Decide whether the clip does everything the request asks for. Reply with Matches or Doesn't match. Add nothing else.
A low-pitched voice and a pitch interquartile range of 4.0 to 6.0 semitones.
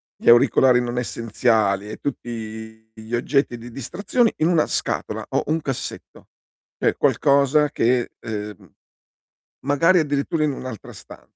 Matches